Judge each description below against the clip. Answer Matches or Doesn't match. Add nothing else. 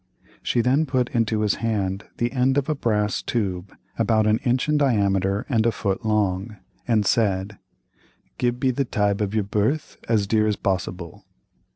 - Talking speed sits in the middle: Matches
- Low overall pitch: Matches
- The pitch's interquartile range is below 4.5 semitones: Matches